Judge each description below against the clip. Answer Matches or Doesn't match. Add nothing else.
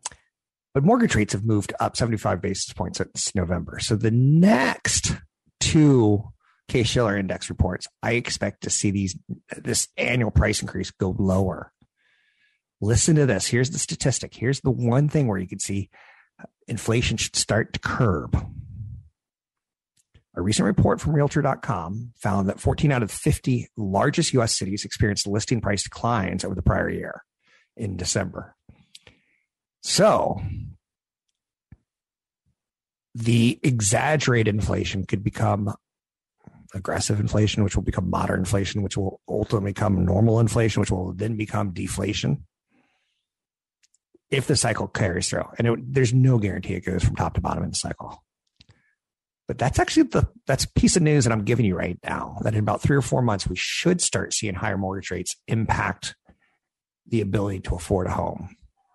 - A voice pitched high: Doesn't match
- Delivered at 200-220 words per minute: Doesn't match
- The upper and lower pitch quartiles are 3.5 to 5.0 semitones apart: Matches